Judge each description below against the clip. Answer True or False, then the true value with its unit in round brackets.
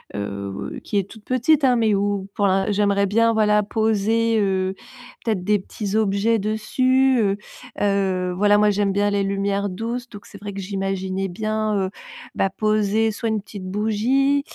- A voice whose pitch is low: False (205 Hz)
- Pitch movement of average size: False (2.0 semitones)